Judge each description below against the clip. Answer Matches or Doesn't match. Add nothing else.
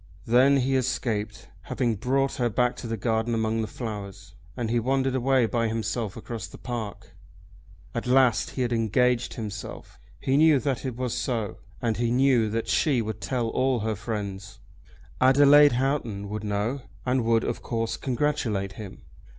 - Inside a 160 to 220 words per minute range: Matches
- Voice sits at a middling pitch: Doesn't match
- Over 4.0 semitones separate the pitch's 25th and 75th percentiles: Doesn't match